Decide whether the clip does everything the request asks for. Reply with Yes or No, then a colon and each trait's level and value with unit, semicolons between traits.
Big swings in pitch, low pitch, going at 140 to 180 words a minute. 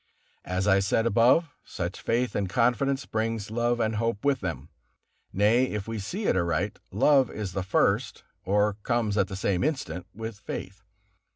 No: average, 3.6 semitones; low, 105 Hz; average, 170 wpm